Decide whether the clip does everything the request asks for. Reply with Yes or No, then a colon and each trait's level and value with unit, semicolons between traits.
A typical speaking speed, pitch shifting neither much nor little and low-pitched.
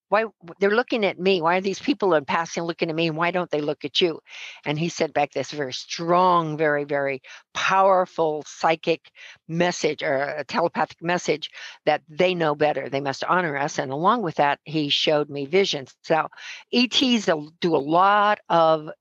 No: average, 185 wpm; average, 3.6 semitones; medium, 165 Hz